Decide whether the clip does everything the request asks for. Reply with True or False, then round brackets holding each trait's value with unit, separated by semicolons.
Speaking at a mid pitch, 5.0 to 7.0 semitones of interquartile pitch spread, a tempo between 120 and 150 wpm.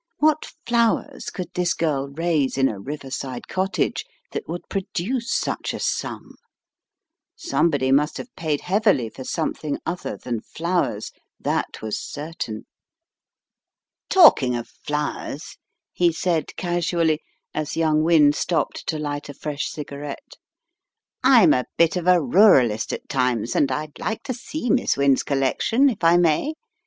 False (155 Hz; 4.5 semitones; 140 wpm)